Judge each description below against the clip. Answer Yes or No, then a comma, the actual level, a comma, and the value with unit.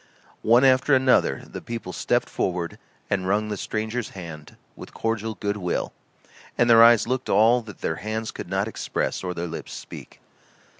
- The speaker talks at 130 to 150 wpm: No, average, 170 wpm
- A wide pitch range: No, average, 3.8 semitones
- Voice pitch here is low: Yes, low, 110 Hz